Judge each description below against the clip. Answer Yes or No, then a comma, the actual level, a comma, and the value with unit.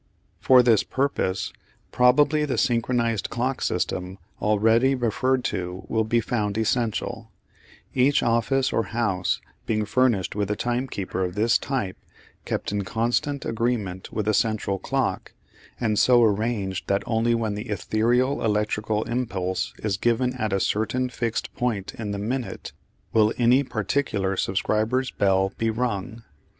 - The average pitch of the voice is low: Yes, low, 110 Hz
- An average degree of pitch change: Yes, average, 3.3 semitones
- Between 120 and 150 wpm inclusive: Yes, average, 140 wpm